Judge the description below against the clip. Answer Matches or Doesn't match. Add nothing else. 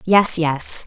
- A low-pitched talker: Doesn't match